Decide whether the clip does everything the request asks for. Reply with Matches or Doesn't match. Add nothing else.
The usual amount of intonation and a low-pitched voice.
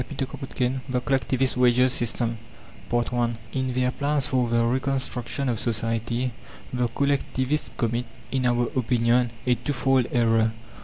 Doesn't match